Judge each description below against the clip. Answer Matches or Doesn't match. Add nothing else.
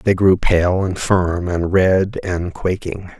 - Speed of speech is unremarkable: Matches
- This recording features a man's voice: Matches